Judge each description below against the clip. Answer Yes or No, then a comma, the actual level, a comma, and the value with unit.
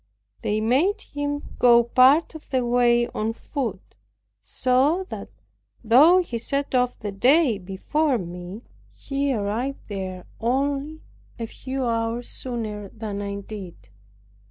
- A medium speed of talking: No, slow, 130 wpm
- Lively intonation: No, average, 4.7 semitones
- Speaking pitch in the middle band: No, high, 240 Hz